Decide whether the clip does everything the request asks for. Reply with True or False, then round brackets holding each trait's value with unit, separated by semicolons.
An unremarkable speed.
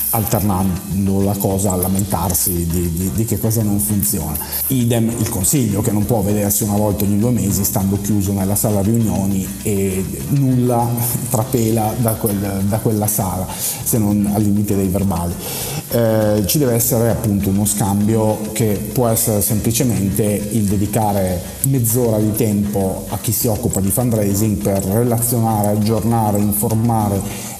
True (150 wpm)